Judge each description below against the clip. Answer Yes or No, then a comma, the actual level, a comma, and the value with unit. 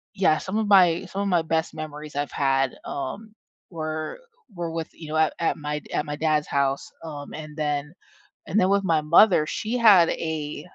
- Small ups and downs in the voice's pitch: No, average, 3.4 semitones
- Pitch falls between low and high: Yes, medium, 160 Hz